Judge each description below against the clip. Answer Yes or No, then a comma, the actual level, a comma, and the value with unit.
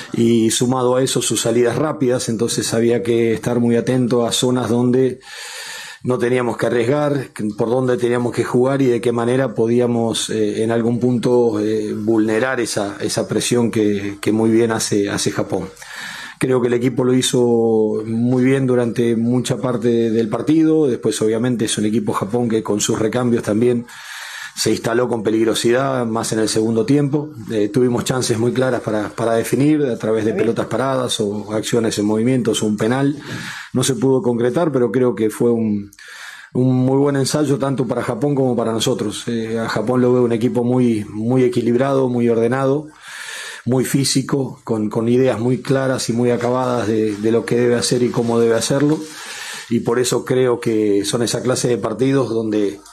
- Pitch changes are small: Yes, narrow, 2.1 semitones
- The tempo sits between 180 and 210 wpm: Yes, average, 185 wpm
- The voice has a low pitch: Yes, low, 120 Hz